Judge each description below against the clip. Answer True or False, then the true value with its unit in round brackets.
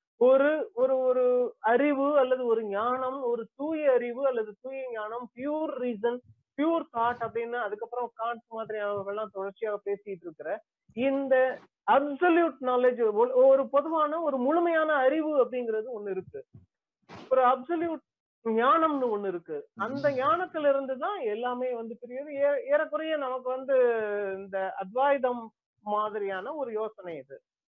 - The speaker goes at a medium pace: True (120 wpm)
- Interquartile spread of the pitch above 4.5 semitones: True (4.9 semitones)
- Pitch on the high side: True (255 Hz)